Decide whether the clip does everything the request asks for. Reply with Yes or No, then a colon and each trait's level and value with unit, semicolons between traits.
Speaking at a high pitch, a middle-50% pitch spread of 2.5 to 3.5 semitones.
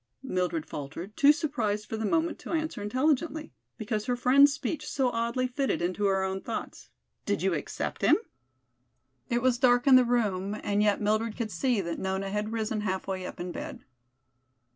No: high, 220 Hz; average, 4.7 semitones